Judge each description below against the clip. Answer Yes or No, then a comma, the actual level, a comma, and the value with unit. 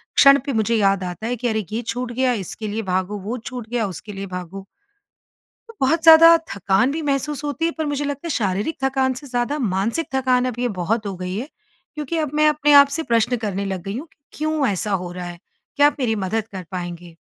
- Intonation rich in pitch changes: Yes, wide, 6.4 semitones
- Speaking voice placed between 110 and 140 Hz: No, high, 240 Hz